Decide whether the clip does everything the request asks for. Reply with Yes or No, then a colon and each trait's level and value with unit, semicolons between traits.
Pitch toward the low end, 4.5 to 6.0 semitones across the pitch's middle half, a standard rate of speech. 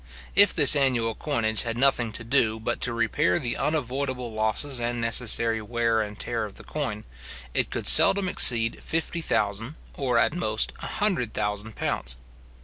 No: low, 115 Hz; average, 3.8 semitones; average, 165 wpm